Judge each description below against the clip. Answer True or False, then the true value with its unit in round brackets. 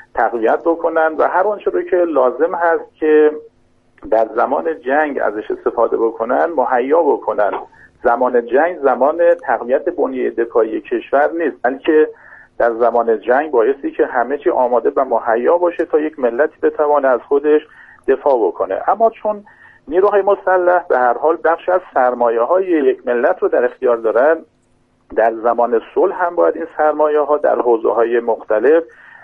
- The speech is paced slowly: False (150 wpm)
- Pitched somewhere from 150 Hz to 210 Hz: True (185 Hz)